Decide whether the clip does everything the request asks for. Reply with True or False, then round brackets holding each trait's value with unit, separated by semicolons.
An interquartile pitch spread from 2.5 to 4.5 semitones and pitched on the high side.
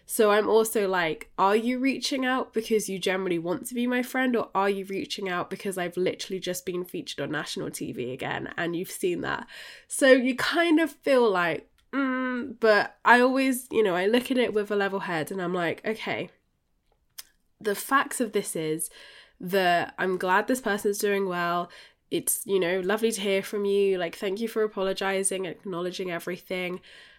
False (4.9 semitones; 200 Hz)